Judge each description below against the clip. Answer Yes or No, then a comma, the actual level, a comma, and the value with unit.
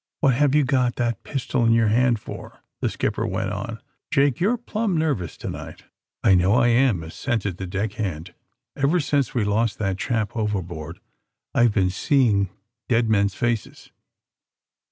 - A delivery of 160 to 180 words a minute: Yes, average, 175 wpm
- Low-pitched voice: Yes, low, 115 Hz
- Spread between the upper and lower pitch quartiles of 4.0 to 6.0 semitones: Yes, average, 5.0 semitones